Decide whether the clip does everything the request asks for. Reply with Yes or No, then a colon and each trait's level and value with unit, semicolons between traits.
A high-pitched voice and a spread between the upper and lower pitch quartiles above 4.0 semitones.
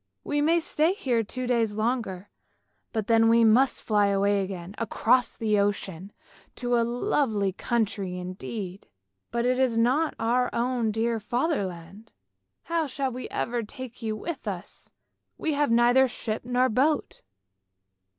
No: high, 230 Hz; average, 3.6 semitones